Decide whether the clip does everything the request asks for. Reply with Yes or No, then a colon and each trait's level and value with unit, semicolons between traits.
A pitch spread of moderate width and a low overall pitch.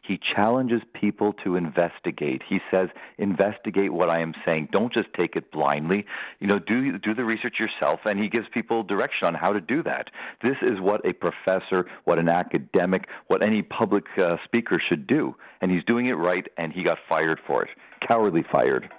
Yes: average, 3.2 semitones; low, 105 Hz